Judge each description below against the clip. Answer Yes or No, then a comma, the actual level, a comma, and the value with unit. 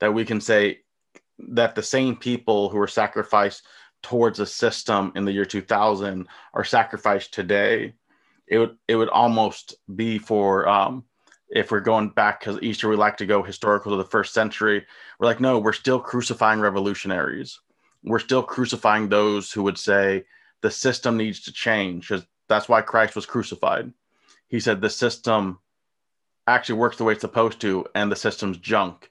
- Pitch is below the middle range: Yes, low, 105 Hz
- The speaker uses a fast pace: No, average, 175 wpm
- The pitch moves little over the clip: Yes, narrow, 2.3 semitones